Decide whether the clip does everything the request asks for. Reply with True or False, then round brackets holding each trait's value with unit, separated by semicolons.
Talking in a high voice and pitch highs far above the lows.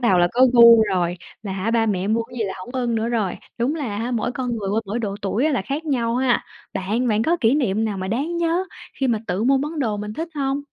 False (230 Hz; 4.2 semitones)